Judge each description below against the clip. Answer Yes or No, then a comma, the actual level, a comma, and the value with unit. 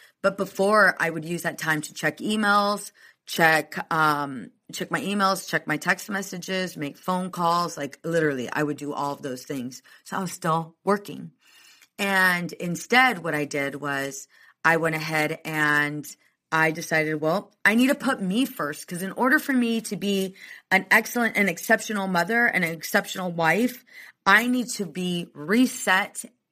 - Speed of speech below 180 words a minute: Yes, average, 170 wpm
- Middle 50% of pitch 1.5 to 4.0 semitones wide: No, average, 4.4 semitones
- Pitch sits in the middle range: Yes, medium, 180 Hz